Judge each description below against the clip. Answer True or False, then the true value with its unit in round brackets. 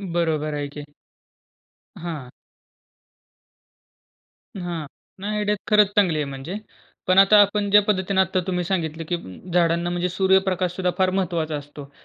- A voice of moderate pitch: True (180 Hz)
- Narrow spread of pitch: False (3.1 semitones)